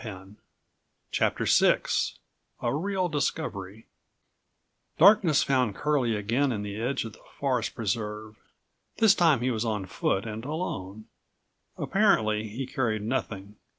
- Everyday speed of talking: No, slow, 120 wpm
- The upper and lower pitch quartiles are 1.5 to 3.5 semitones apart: No, average, 5.2 semitones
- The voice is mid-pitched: No, low, 115 Hz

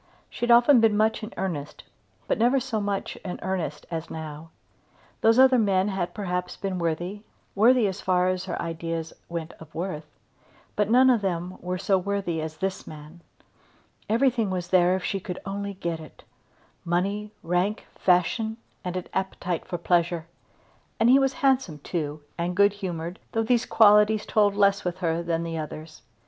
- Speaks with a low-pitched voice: No, medium, 185 Hz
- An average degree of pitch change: Yes, average, 3.7 semitones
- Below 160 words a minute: No, average, 170 wpm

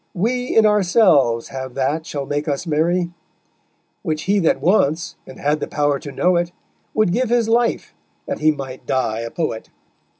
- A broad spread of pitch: Yes, wide, 5.8 semitones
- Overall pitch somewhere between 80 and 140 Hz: No, medium, 160 Hz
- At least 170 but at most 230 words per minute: Yes, average, 175 wpm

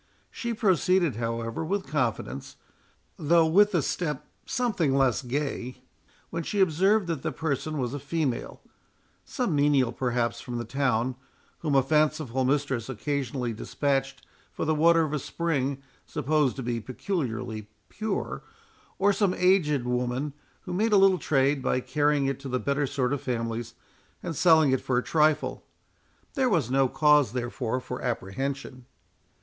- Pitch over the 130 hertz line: Yes, medium, 140 Hz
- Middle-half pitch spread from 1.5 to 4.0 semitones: No, average, 4.4 semitones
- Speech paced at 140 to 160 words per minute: Yes, average, 155 wpm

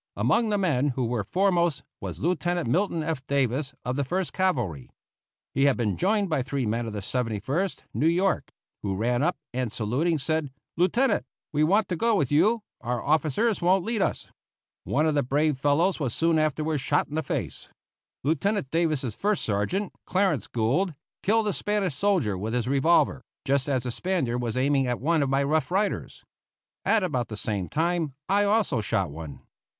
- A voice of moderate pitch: Yes, medium, 150 Hz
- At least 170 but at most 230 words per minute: Yes, average, 185 wpm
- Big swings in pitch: Yes, wide, 6.5 semitones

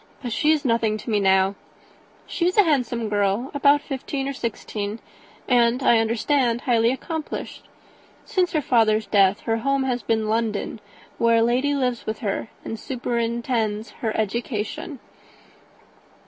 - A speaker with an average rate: Yes, average, 145 wpm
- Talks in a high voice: Yes, high, 235 Hz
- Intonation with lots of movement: No, average, 3.7 semitones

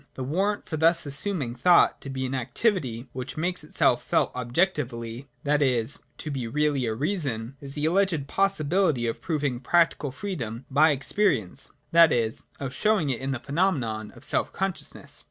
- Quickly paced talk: No, average, 170 wpm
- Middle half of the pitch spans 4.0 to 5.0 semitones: No, wide, 5.4 semitones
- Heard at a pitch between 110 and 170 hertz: Yes, medium, 140 Hz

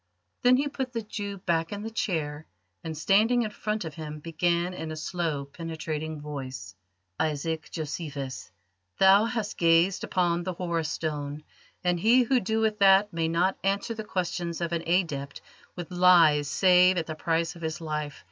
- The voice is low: No, medium, 170 Hz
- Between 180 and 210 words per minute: No, average, 170 wpm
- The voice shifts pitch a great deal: No, average, 3.9 semitones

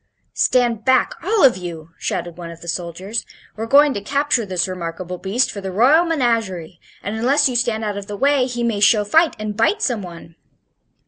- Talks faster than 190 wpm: Yes, average, 200 wpm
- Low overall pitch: No, high, 215 Hz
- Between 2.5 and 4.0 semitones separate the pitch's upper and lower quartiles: No, wide, 5.6 semitones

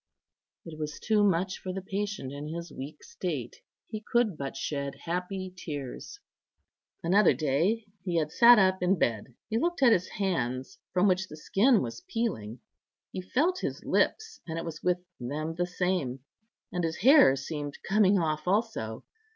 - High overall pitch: No, medium, 180 Hz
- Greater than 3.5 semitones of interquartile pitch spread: Yes, wide, 5.4 semitones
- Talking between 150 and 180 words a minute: Yes, average, 165 wpm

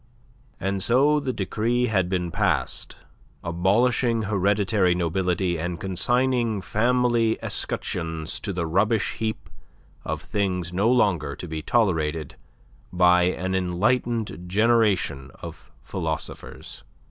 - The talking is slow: Yes, slow, 110 wpm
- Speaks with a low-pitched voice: Yes, very low, 95 Hz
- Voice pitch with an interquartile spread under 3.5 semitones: No, average, 4.4 semitones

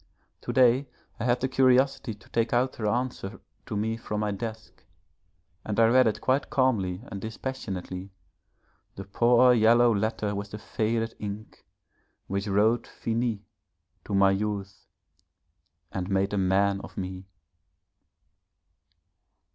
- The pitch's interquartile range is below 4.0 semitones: Yes, average, 3.4 semitones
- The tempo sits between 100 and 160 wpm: Yes, slow, 135 wpm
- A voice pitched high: No, low, 110 Hz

